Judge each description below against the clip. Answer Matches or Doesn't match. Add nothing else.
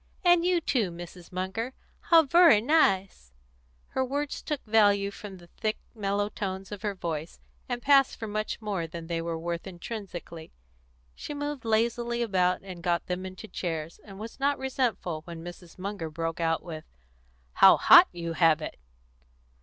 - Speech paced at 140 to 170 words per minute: Matches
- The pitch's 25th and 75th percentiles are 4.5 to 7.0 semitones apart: Matches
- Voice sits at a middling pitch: Doesn't match